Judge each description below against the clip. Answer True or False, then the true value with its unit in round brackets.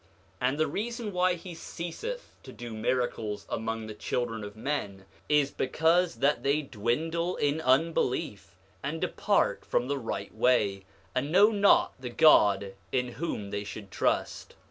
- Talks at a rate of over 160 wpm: False (155 wpm)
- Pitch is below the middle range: True (130 Hz)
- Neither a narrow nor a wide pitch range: False (7.1 semitones)